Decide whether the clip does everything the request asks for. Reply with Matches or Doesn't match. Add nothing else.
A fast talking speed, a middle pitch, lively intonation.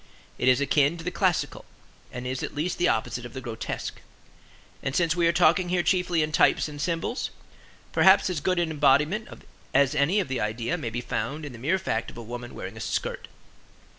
Matches